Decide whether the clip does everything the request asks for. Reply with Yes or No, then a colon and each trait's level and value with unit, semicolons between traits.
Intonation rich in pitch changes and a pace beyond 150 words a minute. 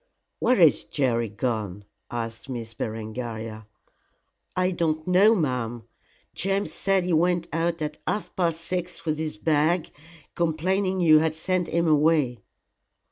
No: wide, 6.6 semitones; slow, 135 wpm